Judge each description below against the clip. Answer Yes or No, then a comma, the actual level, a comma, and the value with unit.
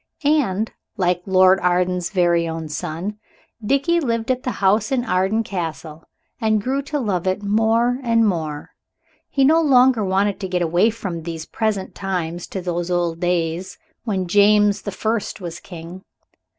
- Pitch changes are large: No, average, 4.3 semitones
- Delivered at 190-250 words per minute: No, average, 160 wpm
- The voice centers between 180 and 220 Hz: Yes, high, 190 Hz